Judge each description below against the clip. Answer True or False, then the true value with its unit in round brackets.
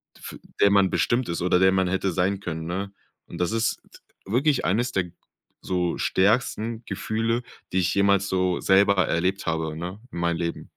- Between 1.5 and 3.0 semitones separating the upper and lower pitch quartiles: True (2.5 semitones)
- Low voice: True (95 Hz)